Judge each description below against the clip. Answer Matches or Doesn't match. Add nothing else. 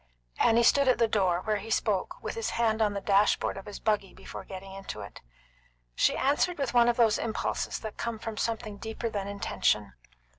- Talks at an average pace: Doesn't match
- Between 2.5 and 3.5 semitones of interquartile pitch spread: Matches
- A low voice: Doesn't match